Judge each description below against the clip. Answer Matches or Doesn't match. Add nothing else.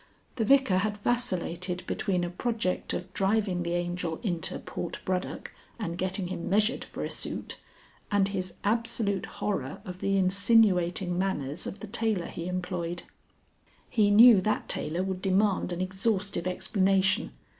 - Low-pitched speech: Doesn't match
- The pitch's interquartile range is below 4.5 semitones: Matches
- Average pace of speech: Matches